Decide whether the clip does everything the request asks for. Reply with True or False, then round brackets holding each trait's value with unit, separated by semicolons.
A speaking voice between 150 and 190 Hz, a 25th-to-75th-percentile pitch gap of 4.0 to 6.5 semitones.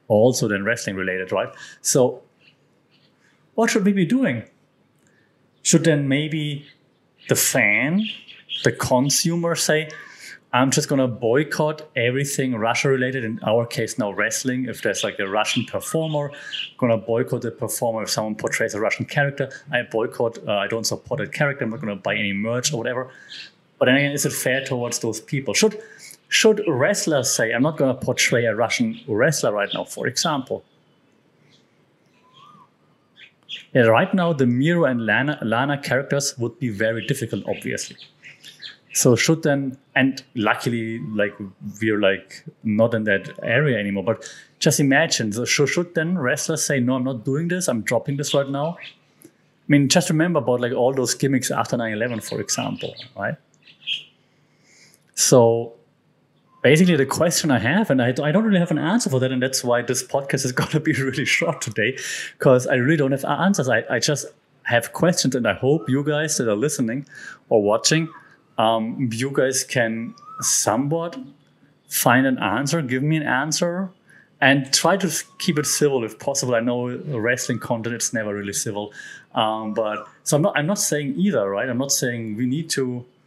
False (135 Hz; 4.7 semitones)